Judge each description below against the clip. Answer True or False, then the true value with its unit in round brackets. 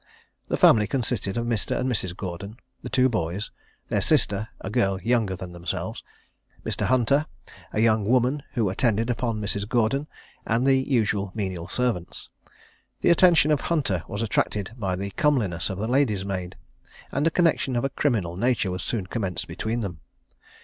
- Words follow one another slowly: False (170 wpm)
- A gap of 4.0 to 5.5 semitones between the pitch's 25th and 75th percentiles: True (4.7 semitones)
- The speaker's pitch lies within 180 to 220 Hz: False (110 Hz)